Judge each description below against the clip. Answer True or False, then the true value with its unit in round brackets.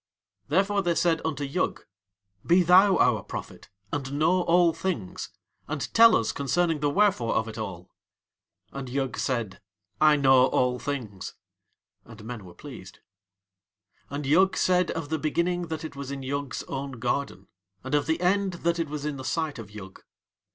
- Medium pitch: True (145 Hz)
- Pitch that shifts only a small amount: False (5.2 semitones)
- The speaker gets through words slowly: False (170 wpm)